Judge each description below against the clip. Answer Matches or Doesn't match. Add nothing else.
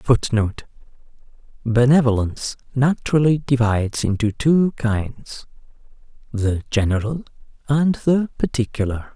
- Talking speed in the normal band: Doesn't match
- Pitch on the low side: Matches